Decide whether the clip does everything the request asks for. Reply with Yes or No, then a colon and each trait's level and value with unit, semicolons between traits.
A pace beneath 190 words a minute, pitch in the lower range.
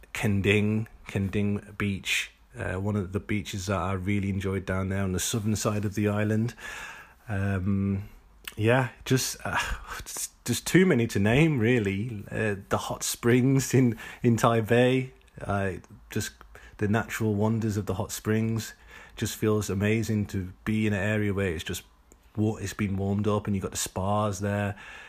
Yes: average, 165 wpm; low, 105 Hz